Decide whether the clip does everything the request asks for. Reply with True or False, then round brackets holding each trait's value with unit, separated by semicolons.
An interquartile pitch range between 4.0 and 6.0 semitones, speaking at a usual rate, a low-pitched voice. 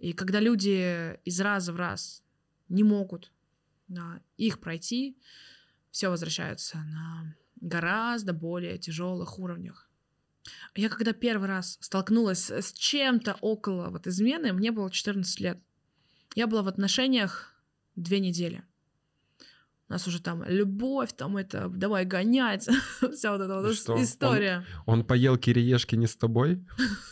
False (4.3 semitones; 130 wpm; 185 Hz)